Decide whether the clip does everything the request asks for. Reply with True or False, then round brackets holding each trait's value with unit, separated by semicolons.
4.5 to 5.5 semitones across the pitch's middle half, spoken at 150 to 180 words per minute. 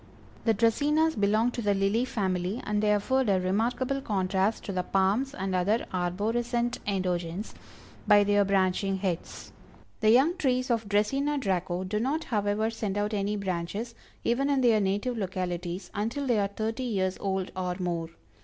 False (3.9 semitones; 165 wpm)